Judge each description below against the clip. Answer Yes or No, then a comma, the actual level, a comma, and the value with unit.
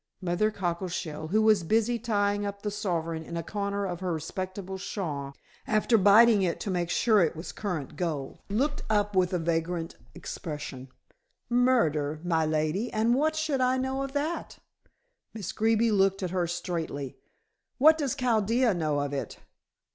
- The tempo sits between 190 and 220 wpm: No, average, 160 wpm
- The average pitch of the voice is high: Yes, high, 195 Hz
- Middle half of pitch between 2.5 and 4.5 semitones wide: No, average, 5.0 semitones